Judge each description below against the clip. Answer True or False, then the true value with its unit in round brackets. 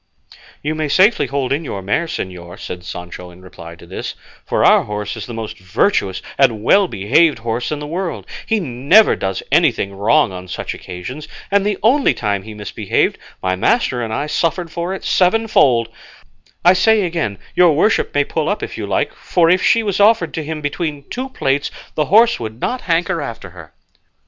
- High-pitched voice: False (145 Hz)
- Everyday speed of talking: True (195 wpm)